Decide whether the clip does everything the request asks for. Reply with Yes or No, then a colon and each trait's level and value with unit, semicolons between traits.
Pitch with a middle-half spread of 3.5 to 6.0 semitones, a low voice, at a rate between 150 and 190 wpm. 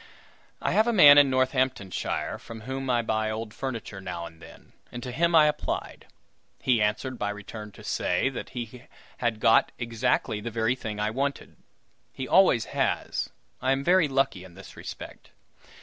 Yes: average, 3.9 semitones; low, 120 Hz; average, 175 wpm